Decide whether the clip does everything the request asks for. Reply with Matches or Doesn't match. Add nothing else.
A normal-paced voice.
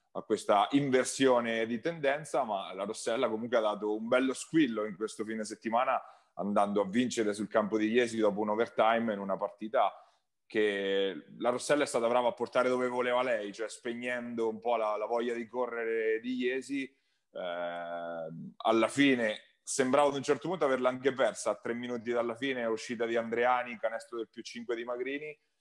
Doesn't match